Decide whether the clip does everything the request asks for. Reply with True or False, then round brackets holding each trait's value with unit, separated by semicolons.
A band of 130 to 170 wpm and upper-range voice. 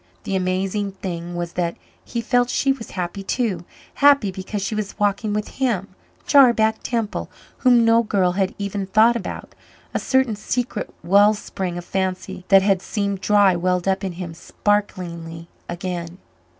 True (160 wpm; 195 Hz)